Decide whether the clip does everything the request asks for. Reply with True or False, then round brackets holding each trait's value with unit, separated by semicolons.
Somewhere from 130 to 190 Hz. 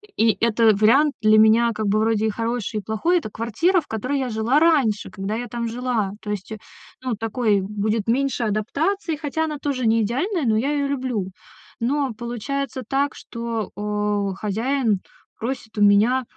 False (230 Hz)